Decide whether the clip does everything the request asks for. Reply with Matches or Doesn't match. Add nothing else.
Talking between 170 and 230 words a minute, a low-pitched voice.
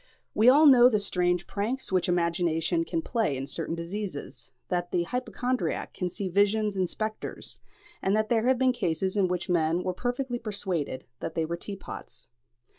Doesn't match